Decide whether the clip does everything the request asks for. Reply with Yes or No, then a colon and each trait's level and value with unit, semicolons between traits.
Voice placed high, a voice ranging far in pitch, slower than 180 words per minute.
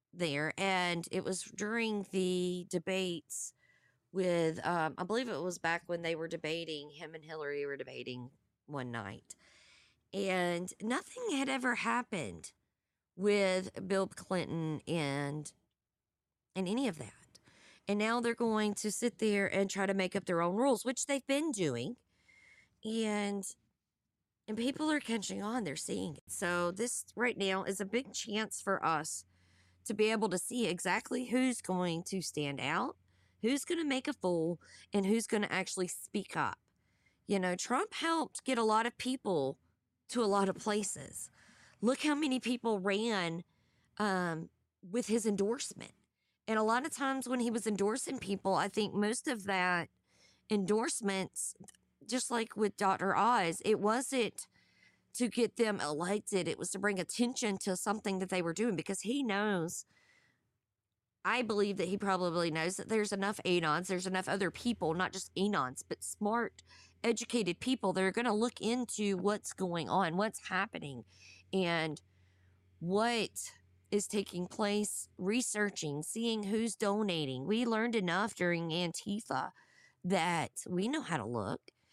No: high, 200 Hz; average, 4.7 semitones; average, 160 wpm